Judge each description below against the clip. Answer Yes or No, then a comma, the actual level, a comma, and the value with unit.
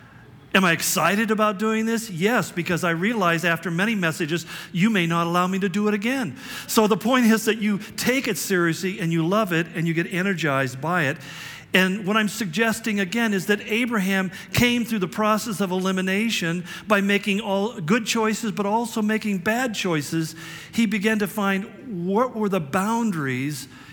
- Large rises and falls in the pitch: No, average, 4.3 semitones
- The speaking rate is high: No, average, 185 wpm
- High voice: Yes, high, 200 Hz